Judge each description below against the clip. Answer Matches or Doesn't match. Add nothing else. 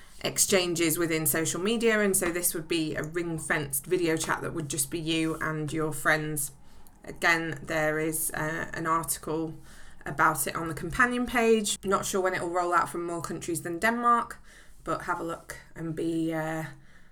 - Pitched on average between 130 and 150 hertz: Doesn't match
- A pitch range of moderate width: Doesn't match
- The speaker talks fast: Doesn't match